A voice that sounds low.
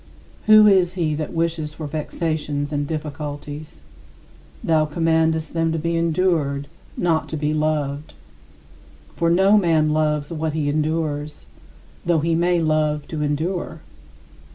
No: medium, 155 Hz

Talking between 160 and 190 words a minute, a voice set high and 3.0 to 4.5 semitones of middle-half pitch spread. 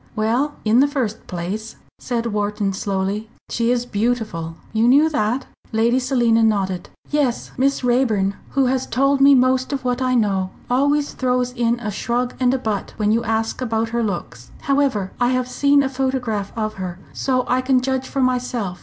Yes: average, 180 wpm; high, 240 Hz; average, 3.3 semitones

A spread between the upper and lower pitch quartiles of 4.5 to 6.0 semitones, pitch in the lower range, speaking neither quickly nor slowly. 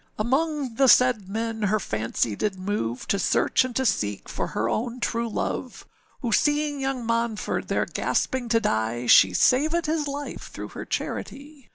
No: wide, 5.5 semitones; high, 230 Hz; average, 170 wpm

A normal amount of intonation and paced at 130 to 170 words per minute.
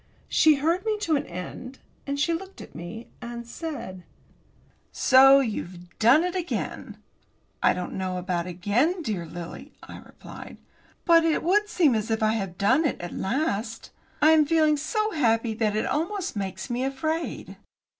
No: wide, 7.9 semitones; average, 165 wpm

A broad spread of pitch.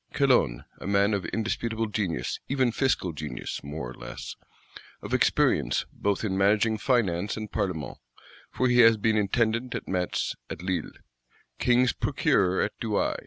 No: average, 4.1 semitones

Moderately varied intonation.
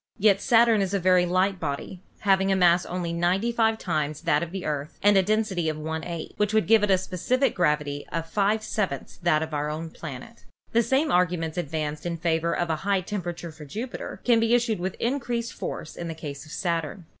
Yes: average, 4.6 semitones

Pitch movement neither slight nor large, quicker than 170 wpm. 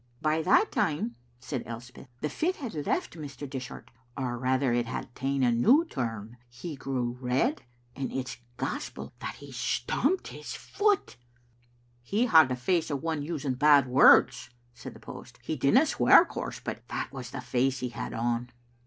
Yes: average, 3.9 semitones; average, 180 wpm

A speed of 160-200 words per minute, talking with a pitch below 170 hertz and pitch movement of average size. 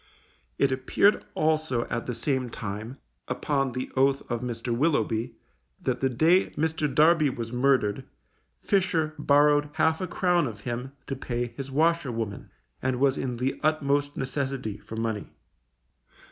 No: average, 145 wpm; low, 135 Hz; average, 4.0 semitones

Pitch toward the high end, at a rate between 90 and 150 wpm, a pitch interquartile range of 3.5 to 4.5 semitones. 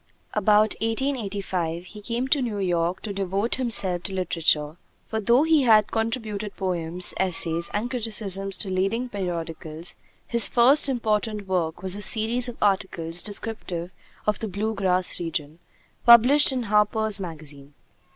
Yes: high, 200 Hz; average, 140 wpm; average, 4.1 semitones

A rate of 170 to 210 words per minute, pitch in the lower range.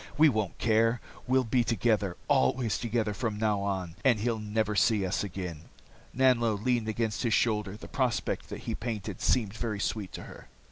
Yes: average, 180 wpm; low, 110 Hz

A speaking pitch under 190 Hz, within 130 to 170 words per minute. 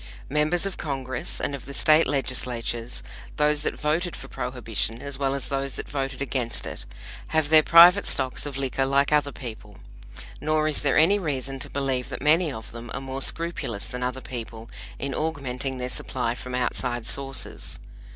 No: low, 135 Hz; average, 180 wpm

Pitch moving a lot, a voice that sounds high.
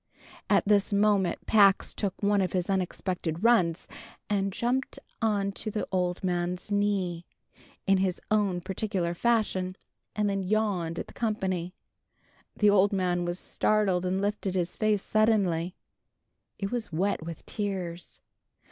No: narrow, 2.6 semitones; high, 195 Hz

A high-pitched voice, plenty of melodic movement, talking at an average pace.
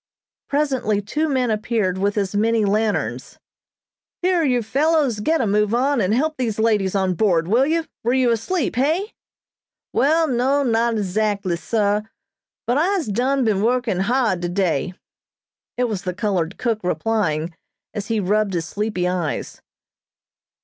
No: high, 220 Hz; average, 4.7 semitones; average, 150 wpm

